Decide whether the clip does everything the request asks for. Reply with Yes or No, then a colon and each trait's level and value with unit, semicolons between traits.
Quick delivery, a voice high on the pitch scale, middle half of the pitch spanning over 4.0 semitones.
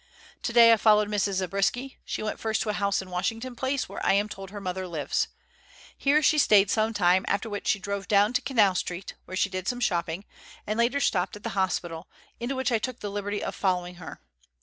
No: fast, 220 wpm; high, 205 Hz; average, 3.4 semitones